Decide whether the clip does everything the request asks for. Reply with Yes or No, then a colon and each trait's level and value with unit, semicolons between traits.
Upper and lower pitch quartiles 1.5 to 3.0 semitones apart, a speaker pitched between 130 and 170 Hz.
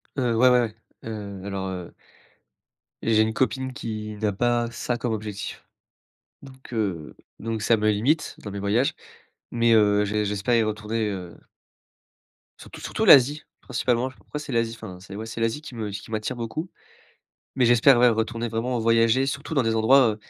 No: narrow, 2.6 semitones; low, 115 Hz